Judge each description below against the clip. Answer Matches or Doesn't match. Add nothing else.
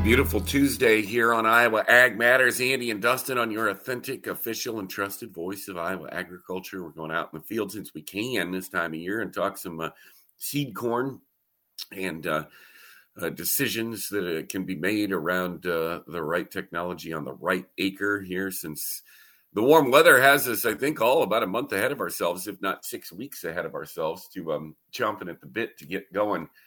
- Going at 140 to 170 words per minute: Doesn't match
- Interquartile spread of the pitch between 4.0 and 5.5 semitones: Matches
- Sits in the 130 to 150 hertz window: Doesn't match